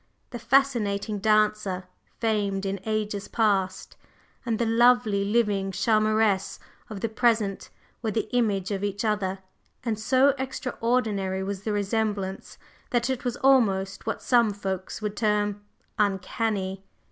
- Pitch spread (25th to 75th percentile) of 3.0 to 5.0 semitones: No, narrow, 2.5 semitones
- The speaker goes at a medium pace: No, slow, 130 wpm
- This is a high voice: Yes, high, 210 Hz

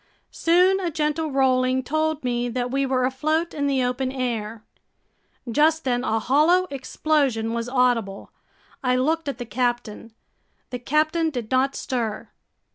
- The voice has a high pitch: Yes, very high, 260 Hz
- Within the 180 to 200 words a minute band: No, average, 145 wpm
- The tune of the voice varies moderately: Yes, average, 3.9 semitones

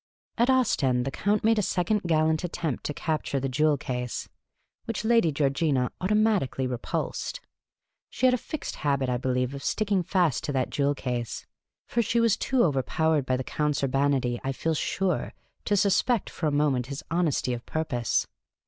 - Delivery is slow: No, average, 175 wpm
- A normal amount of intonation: No, wide, 7.1 semitones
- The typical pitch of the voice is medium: Yes, medium, 150 Hz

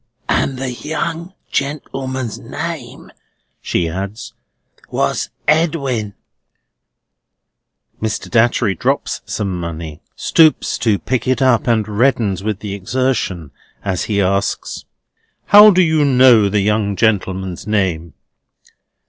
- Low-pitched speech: Yes, low, 110 Hz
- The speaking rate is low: Yes, slow, 110 wpm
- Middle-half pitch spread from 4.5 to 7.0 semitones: Yes, average, 5.2 semitones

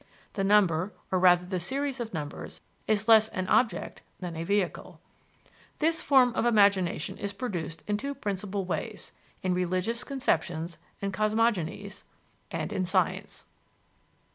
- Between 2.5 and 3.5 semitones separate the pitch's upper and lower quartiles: No, average, 3.9 semitones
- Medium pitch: No, high, 200 Hz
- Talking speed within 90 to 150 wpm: Yes, average, 140 wpm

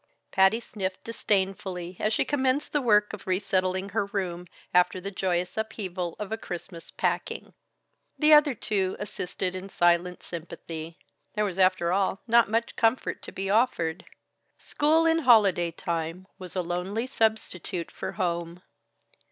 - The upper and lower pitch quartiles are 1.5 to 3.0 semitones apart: No, average, 3.6 semitones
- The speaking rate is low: No, average, 145 wpm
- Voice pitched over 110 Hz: Yes, high, 190 Hz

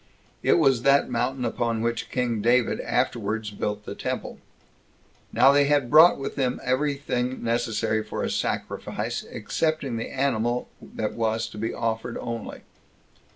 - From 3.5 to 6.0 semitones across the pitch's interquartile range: No, average, 3.1 semitones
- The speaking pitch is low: Yes, low, 120 Hz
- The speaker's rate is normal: Yes, average, 155 wpm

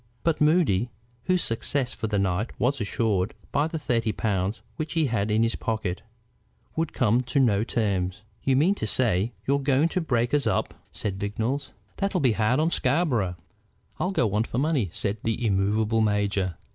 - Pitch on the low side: Yes, low, 115 Hz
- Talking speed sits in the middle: Yes, average, 180 wpm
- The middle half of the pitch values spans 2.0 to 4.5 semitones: No, wide, 5.5 semitones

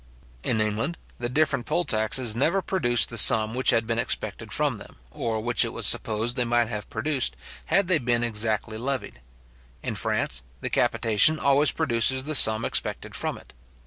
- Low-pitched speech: Yes, low, 120 Hz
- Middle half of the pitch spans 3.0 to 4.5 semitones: Yes, average, 3.9 semitones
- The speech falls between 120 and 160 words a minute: No, average, 175 wpm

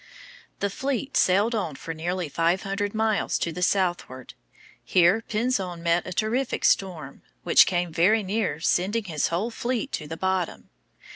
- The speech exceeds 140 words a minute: Yes, average, 155 wpm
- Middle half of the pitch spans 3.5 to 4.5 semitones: Yes, average, 4.2 semitones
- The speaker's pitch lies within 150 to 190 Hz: Yes, medium, 185 Hz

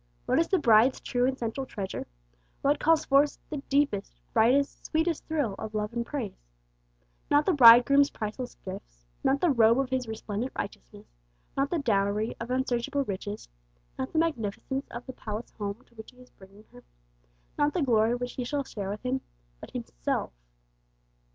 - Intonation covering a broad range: No, average, 4.6 semitones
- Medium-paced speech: Yes, average, 175 wpm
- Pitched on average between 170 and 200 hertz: No, high, 245 Hz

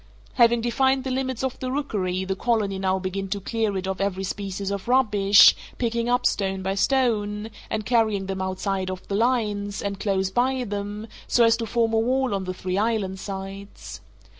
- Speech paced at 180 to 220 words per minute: Yes, average, 190 wpm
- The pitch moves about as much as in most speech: Yes, average, 3.5 semitones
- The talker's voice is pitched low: No, high, 205 Hz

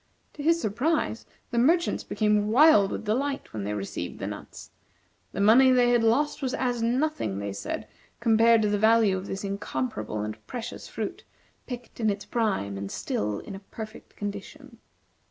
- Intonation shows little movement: No, average, 4.2 semitones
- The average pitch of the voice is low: No, high, 220 Hz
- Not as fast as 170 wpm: No, average, 175 wpm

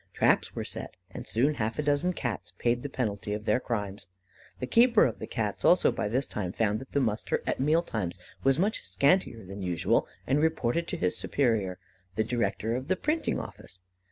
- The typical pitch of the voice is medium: No, low, 120 Hz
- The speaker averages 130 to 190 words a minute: No, average, 200 wpm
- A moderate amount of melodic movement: No, wide, 5.8 semitones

